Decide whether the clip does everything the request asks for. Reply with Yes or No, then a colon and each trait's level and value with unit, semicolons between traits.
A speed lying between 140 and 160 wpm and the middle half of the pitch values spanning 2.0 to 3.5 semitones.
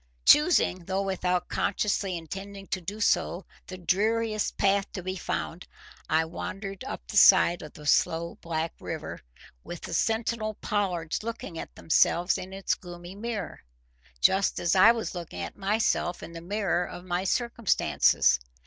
Yes: average, 155 wpm; average, 3.0 semitones